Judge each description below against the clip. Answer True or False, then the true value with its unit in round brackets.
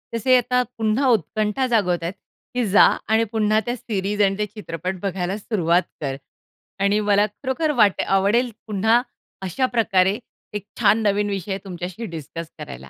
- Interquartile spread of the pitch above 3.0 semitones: True (3.4 semitones)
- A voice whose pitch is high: True (205 Hz)